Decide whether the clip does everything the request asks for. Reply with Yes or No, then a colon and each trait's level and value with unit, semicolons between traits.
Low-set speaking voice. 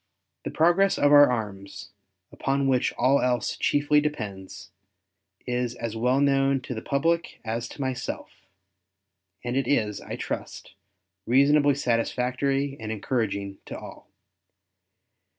Yes: low, 125 Hz